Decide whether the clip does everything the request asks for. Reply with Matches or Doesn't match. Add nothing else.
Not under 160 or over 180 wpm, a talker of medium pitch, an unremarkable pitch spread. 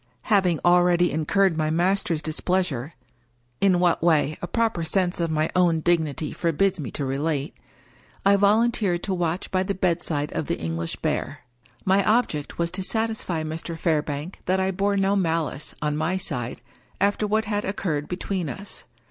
Matches